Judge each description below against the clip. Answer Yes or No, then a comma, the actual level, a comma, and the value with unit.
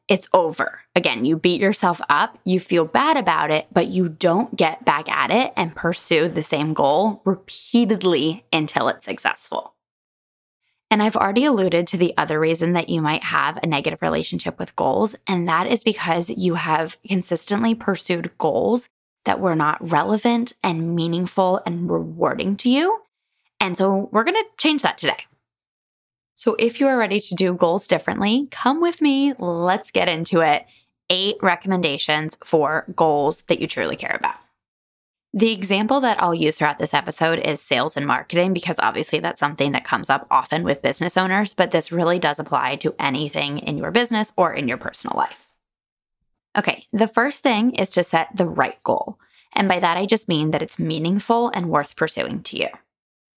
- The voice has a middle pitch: Yes, medium, 180 Hz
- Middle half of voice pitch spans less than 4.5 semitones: No, average, 5.2 semitones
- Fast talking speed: No, average, 180 wpm